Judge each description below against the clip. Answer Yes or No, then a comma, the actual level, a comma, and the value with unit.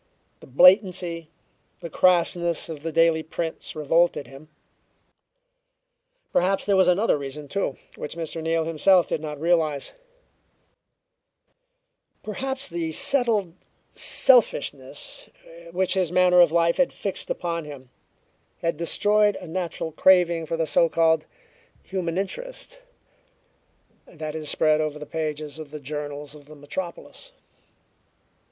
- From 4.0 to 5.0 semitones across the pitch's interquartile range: No, average, 3.1 semitones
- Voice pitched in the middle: Yes, medium, 165 Hz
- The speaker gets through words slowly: Yes, slow, 125 wpm